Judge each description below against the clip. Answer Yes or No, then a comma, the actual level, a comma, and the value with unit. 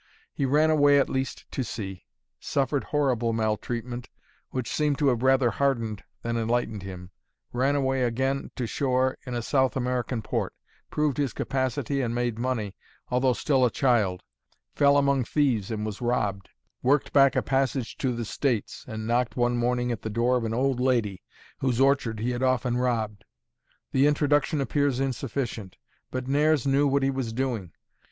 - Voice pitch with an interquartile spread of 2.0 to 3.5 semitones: Yes, average, 2.9 semitones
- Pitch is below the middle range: Yes, low, 125 Hz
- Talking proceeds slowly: No, average, 170 wpm